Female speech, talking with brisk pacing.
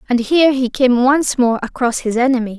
Yes: female; fast, 210 wpm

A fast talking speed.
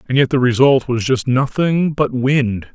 No: average, 195 wpm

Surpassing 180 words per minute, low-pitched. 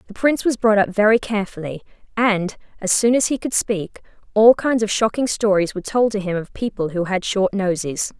No: fast, 205 wpm; high, 210 Hz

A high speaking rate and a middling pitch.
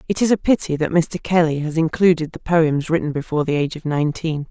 Yes: fast, 225 wpm; medium, 160 Hz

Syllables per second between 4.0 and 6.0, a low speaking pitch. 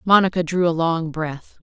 No: 4.7 syllables/s; medium, 170 Hz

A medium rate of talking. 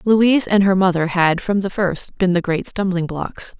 No: fast, 215 wpm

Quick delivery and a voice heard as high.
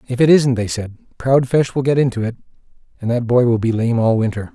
No: fast, 250 wpm; low, 125 Hz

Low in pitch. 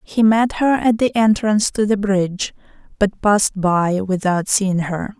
No: high, 205 Hz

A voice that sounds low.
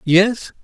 No: high, 200 Hz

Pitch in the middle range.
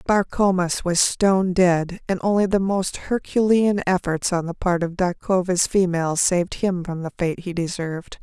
Yes: medium, 180 Hz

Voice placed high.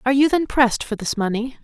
Yes: very high, 250 Hz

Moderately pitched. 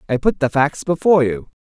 Yes: medium, 145 Hz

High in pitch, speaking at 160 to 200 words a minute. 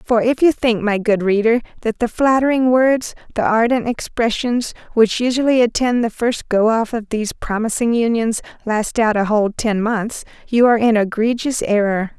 Yes: high, 230 Hz; average, 175 wpm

